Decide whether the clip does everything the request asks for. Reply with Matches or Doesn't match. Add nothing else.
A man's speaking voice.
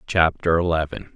Matches